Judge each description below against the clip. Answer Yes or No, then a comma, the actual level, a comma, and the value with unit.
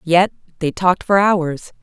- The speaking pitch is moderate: Yes, medium, 175 Hz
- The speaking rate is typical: Yes, average, 165 wpm